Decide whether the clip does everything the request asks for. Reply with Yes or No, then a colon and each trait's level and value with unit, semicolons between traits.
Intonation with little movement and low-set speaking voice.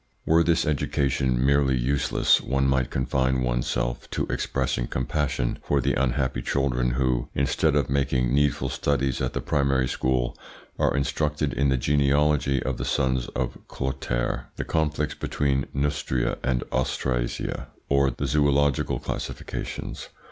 Yes: narrow, 1.9 semitones; very low, 65 Hz